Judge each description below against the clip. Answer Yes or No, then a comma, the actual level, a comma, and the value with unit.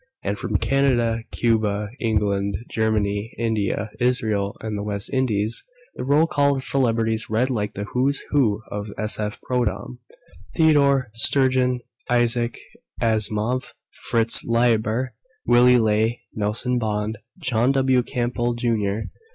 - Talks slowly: Yes, slow, 120 wpm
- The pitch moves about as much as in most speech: Yes, average, 3.0 semitones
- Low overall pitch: Yes, low, 115 Hz